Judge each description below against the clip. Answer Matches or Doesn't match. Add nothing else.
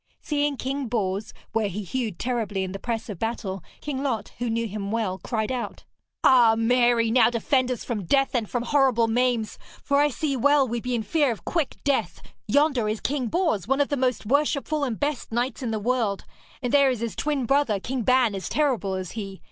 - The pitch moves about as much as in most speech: Matches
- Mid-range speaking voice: Doesn't match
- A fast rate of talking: Matches